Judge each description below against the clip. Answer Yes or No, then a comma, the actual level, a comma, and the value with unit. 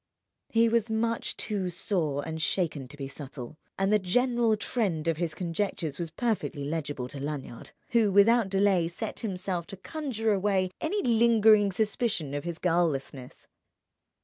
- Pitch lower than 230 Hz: Yes, medium, 185 Hz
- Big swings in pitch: Yes, wide, 5.7 semitones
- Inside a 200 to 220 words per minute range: No, average, 150 wpm